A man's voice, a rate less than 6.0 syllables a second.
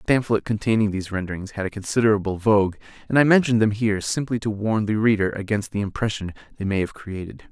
No: male; 6.7 syllables/s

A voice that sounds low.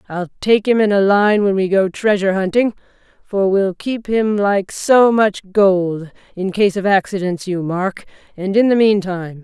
No: high, 195 Hz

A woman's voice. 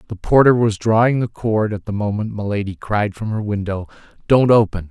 No: male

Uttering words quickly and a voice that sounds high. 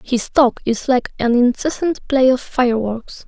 No: average, 165 wpm; very high, 250 Hz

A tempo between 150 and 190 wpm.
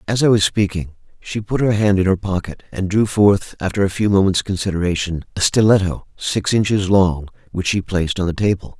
No: fast, 205 wpm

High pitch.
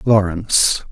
No: very low, 95 Hz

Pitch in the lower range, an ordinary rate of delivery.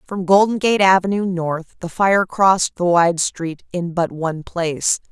No: medium, 180 Hz; average, 175 wpm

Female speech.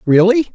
No: male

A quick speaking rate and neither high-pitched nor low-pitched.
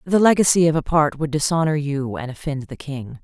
Yes: fast, 225 wpm; medium, 150 Hz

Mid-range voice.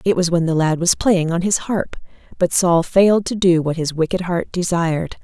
Yes: medium, 175 Hz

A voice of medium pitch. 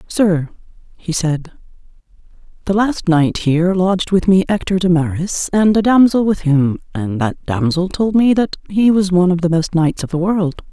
Yes: medium, 180 Hz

